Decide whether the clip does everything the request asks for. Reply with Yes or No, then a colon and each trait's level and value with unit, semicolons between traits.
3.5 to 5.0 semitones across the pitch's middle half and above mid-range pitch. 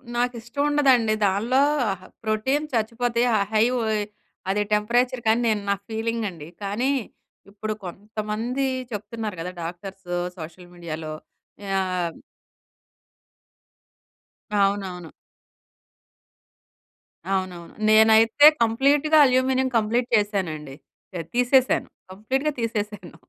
Yes: average, 4.0 semitones; high, 215 Hz